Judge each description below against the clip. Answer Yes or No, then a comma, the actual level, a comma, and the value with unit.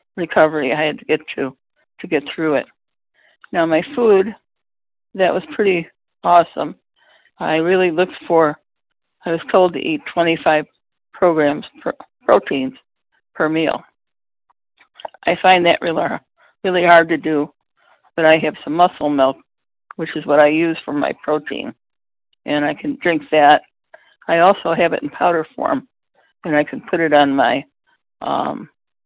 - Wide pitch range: No, average, 3.0 semitones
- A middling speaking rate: Yes, average, 155 wpm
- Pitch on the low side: No, medium, 160 Hz